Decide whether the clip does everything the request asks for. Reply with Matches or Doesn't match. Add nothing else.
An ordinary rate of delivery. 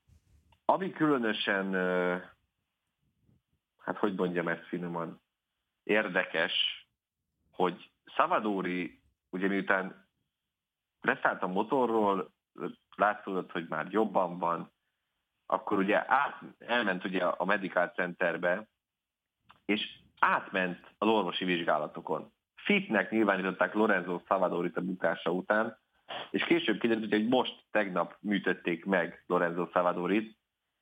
Doesn't match